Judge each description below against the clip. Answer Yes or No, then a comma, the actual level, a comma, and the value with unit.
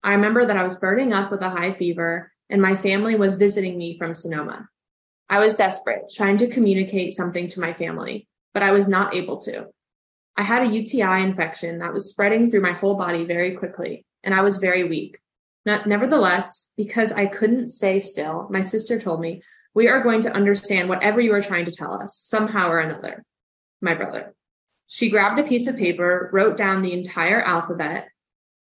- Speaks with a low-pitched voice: No, high, 195 Hz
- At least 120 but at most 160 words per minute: No, average, 195 wpm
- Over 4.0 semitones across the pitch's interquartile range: No, average, 3.1 semitones